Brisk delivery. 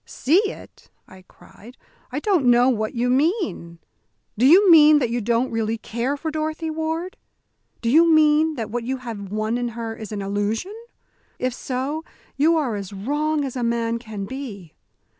No: average, 180 wpm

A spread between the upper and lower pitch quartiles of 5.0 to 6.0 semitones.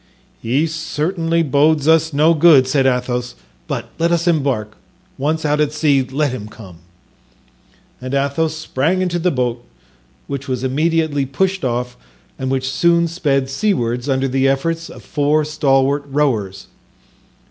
No: average, 3.6 semitones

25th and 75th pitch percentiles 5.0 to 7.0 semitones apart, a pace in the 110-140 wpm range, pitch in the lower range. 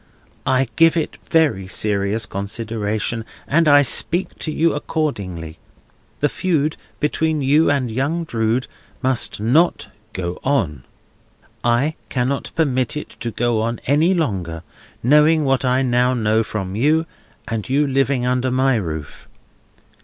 Yes: wide, 5.4 semitones; slow, 135 wpm; low, 130 Hz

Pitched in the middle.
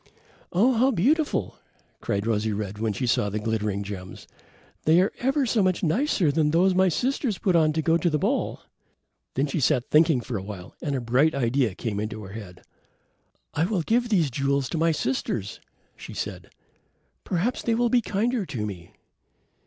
Yes: medium, 150 Hz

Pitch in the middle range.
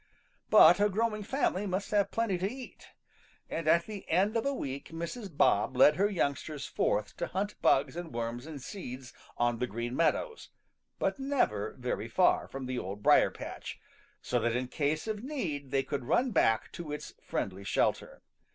Yes: medium, 155 Hz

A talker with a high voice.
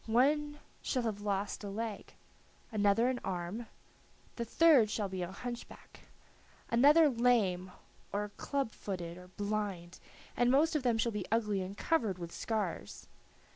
Yes: high, 215 Hz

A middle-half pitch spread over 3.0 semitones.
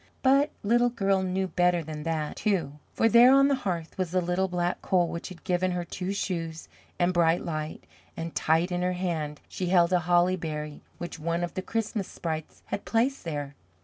No: narrow, 2.5 semitones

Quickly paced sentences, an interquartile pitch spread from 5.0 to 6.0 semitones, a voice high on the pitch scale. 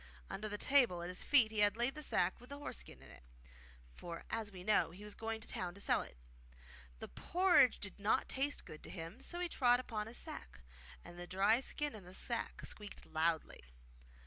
Yes: fast, 225 wpm; wide, 5.5 semitones; high, 210 Hz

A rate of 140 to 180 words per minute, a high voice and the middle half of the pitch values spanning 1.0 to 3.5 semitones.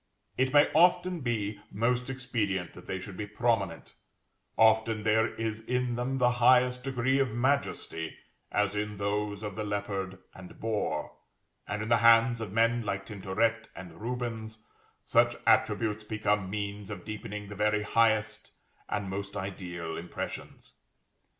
No: average, 145 wpm; low, 110 Hz; average, 2.8 semitones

